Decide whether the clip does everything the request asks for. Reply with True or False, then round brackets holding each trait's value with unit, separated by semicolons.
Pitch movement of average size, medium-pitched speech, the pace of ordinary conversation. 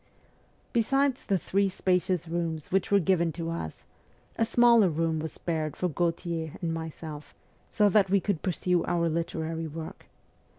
True (3.0 semitones; 170 Hz; 155 wpm)